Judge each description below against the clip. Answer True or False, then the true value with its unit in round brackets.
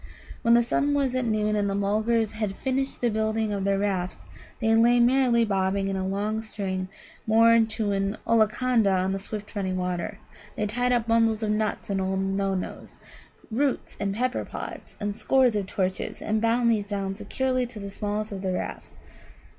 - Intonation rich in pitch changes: False (2.8 semitones)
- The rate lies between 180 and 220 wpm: True (185 wpm)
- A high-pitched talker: True (215 Hz)